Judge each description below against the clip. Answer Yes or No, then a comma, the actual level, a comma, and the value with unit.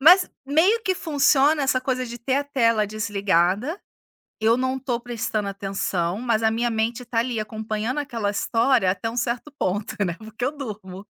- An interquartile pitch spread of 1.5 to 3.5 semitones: No, average, 3.9 semitones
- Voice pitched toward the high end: Yes, high, 230 Hz